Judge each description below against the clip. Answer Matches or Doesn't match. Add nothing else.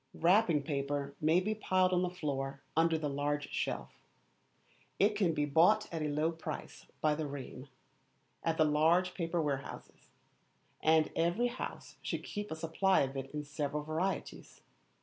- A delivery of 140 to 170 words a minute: Matches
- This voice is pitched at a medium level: Matches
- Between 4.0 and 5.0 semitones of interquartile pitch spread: Doesn't match